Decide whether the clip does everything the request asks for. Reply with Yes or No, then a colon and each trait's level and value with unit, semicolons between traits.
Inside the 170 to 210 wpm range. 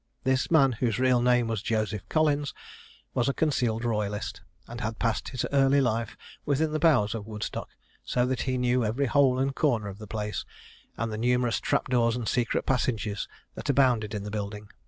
Yes: average, 190 wpm